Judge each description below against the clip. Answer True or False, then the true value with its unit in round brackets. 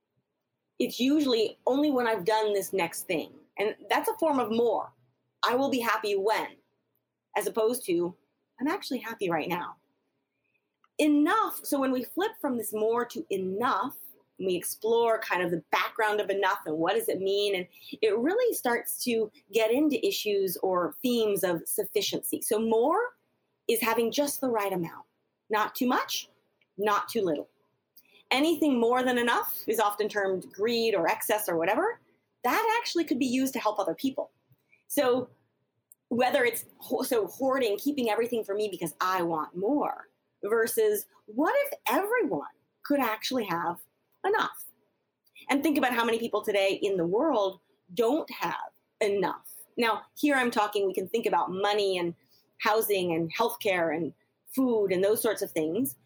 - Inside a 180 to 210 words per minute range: False (165 wpm)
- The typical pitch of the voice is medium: False (230 Hz)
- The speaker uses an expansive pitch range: True (6.3 semitones)